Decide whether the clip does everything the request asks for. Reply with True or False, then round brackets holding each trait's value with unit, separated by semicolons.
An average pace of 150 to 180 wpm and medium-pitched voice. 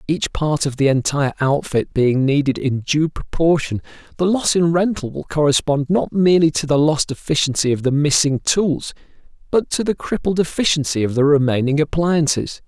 True (170 wpm; 150 Hz)